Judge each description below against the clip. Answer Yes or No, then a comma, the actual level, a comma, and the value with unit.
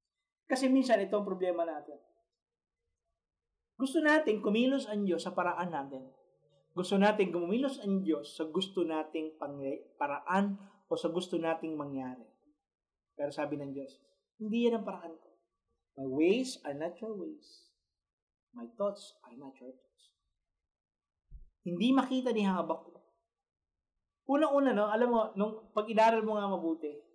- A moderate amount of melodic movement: No, wide, 6.4 semitones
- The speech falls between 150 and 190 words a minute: No, slow, 135 wpm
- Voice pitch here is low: No, high, 190 Hz